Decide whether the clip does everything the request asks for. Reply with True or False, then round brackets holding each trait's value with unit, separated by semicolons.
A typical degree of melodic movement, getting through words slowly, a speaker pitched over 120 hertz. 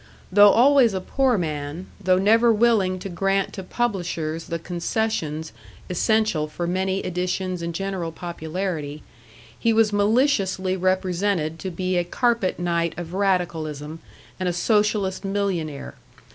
True (3.3 semitones; 130 wpm; 185 Hz)